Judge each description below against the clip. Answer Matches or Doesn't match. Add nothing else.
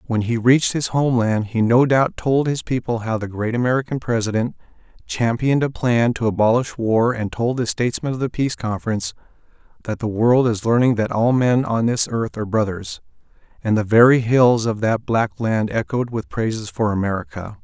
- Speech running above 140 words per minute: Matches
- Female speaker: Doesn't match